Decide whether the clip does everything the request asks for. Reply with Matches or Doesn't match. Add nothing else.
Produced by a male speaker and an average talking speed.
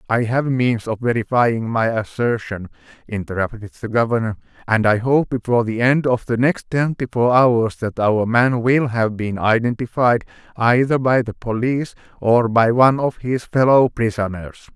Matches